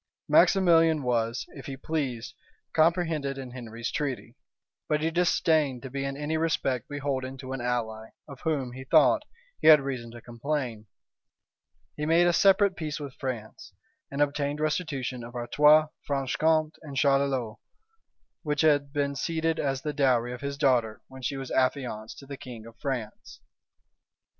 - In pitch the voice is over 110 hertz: Yes, medium, 140 Hz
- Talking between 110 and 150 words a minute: No, average, 160 wpm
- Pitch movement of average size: Yes, average, 3.6 semitones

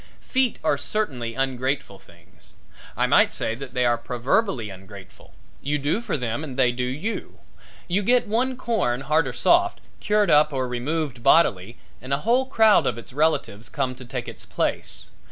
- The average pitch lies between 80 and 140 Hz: Yes, low, 135 Hz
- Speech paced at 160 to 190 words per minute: Yes, average, 175 wpm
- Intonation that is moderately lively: No, wide, 8.9 semitones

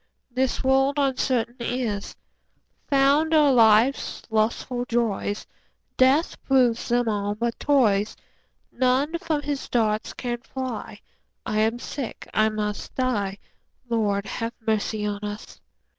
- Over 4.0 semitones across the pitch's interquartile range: No, average, 3.7 semitones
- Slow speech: Yes, slow, 125 wpm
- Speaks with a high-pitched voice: Yes, high, 240 Hz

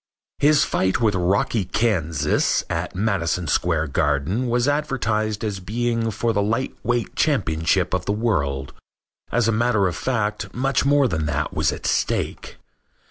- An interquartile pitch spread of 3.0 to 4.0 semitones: No, average, 5.3 semitones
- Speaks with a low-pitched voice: Yes, low, 105 Hz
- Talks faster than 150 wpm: No, average, 145 wpm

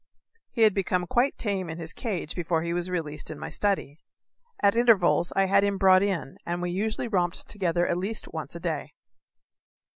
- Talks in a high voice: No, medium, 180 Hz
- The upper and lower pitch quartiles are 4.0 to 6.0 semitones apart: No, average, 3.0 semitones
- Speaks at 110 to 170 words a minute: No, average, 190 wpm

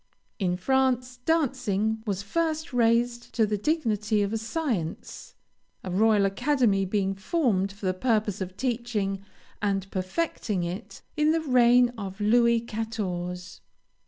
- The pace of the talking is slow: Yes, slow, 130 wpm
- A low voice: No, high, 220 Hz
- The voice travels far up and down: No, average, 4.1 semitones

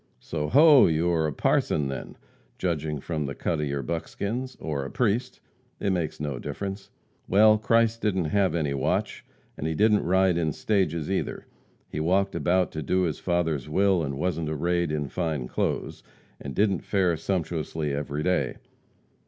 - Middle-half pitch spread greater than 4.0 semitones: Yes, average, 4.4 semitones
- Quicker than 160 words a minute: Yes, average, 170 wpm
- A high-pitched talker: No, very low, 85 Hz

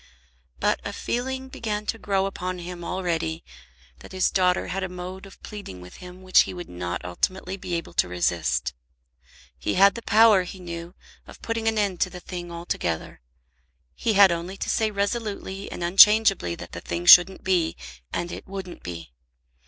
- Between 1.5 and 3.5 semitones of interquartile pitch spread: Yes, average, 2.8 semitones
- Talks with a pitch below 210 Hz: Yes, medium, 185 Hz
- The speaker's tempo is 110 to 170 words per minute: No, average, 180 wpm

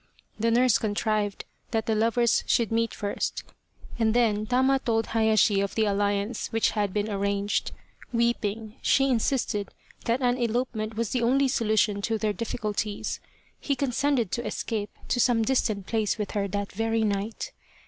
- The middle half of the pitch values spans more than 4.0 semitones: No, narrow, 2.4 semitones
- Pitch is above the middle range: Yes, high, 220 Hz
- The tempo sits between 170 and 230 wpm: No, average, 160 wpm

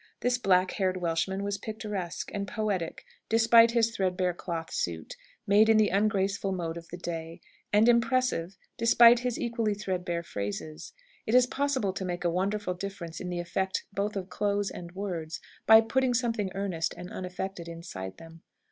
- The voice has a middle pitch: No, high, 195 Hz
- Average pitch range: Yes, average, 4.0 semitones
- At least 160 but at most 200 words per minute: Yes, average, 165 wpm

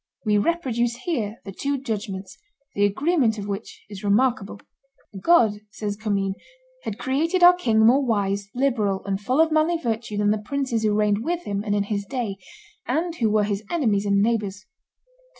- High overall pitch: Yes, high, 220 Hz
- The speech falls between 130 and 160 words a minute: No, average, 175 wpm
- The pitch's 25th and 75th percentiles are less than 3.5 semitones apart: No, average, 4.6 semitones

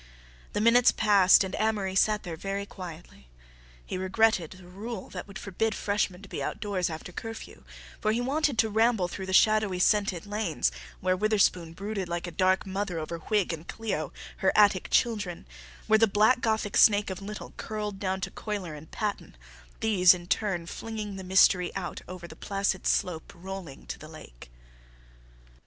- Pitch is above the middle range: Yes, high, 195 Hz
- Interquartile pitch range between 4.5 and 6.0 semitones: No, average, 3.0 semitones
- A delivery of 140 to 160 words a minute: No, average, 175 wpm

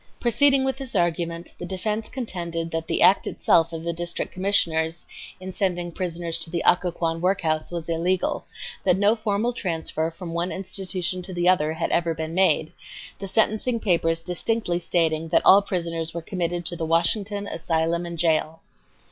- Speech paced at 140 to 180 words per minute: Yes, average, 165 wpm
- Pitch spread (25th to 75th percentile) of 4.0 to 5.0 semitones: No, narrow, 2.6 semitones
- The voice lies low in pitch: No, medium, 175 Hz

